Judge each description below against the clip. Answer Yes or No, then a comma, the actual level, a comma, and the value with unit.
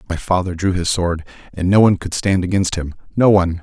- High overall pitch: No, very low, 90 Hz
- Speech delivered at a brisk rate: Yes, fast, 215 wpm